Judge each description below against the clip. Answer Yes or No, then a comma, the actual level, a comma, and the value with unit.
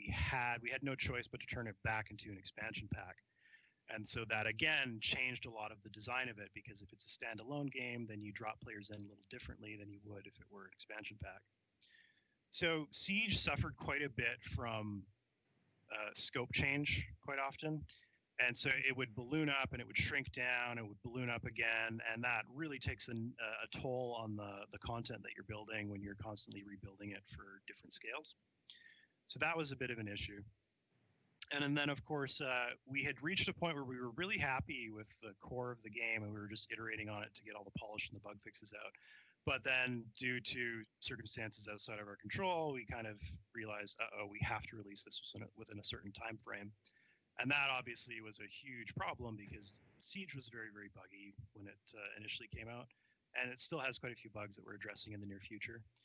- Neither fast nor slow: No, fast, 220 wpm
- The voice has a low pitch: Yes, low, 115 Hz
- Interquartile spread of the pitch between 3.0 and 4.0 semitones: Yes, average, 3.4 semitones